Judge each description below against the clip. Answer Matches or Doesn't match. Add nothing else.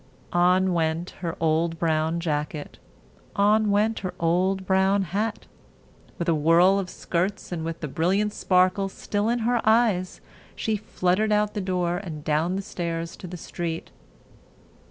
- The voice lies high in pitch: Doesn't match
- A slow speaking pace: Doesn't match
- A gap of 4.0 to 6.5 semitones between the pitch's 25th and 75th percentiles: Doesn't match